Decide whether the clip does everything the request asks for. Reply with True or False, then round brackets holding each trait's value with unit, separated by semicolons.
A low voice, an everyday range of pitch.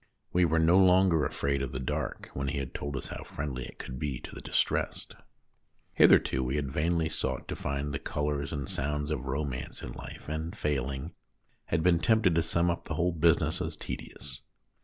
True (75 Hz; 3.5 semitones)